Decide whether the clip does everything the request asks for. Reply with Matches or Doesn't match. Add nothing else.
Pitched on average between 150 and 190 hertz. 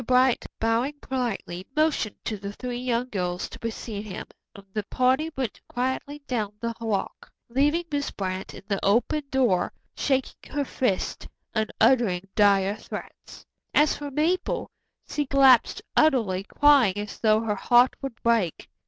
Doesn't match